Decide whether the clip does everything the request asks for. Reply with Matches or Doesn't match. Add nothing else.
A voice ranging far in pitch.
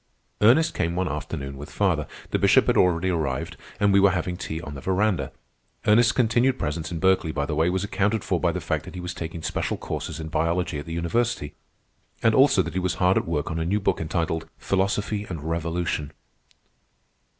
Doesn't match